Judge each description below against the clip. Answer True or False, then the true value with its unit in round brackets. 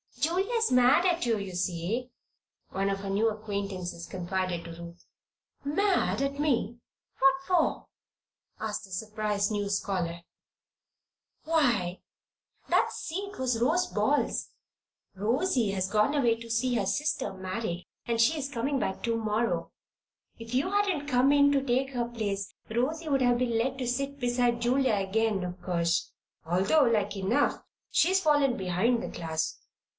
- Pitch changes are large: True (5.8 semitones)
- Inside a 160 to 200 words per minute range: False (145 wpm)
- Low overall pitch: False (230 Hz)